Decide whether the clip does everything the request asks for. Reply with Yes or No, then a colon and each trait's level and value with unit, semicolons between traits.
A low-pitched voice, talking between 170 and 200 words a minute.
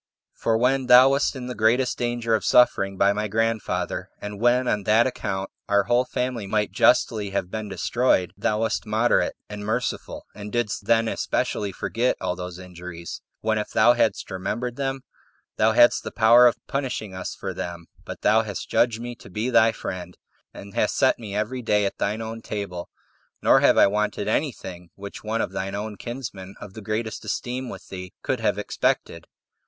Yes: low, 110 Hz; average, 190 wpm